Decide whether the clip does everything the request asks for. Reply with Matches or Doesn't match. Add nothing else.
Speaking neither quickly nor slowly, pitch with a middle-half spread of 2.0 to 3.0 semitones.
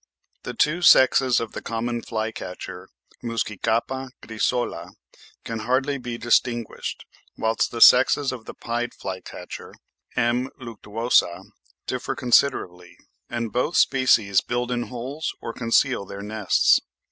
Doesn't match